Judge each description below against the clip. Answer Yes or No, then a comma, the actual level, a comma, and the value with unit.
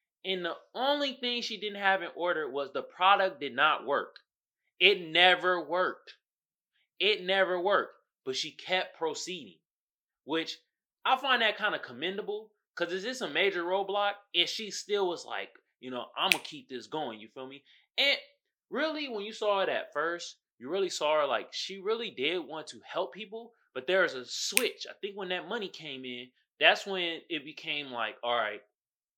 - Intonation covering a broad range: Yes, wide, 5.9 semitones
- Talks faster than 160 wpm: Yes, average, 190 wpm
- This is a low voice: No, high, 190 Hz